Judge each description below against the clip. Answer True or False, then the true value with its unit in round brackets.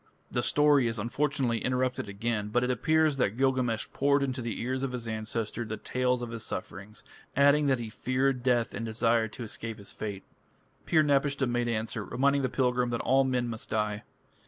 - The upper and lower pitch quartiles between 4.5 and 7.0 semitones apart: False (2.9 semitones)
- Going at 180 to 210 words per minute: True (190 wpm)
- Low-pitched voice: True (120 Hz)